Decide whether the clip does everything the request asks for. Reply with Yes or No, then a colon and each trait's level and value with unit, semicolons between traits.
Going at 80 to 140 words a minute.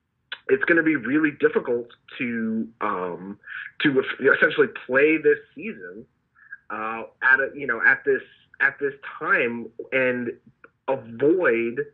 Yes: slow, 135 wpm